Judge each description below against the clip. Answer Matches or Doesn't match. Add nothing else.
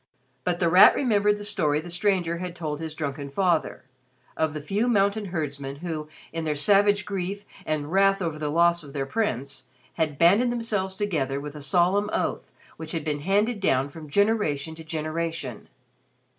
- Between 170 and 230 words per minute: Matches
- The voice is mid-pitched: Matches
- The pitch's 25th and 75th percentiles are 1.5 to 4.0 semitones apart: Doesn't match